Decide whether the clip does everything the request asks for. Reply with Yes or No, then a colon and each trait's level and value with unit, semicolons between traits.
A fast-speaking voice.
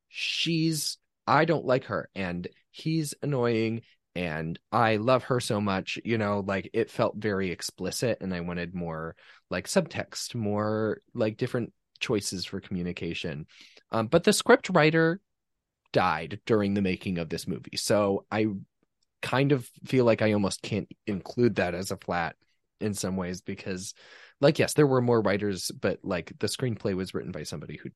No: average, 165 wpm